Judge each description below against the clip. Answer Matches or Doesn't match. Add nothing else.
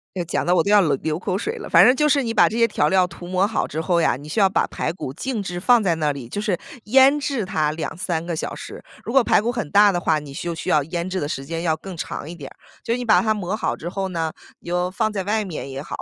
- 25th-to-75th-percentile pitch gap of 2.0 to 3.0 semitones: Doesn't match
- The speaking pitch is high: Doesn't match